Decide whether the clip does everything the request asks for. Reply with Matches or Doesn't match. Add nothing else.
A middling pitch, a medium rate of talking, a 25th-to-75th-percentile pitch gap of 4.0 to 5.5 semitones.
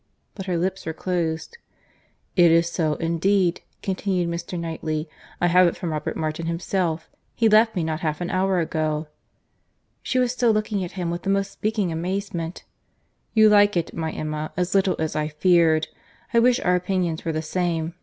Doesn't match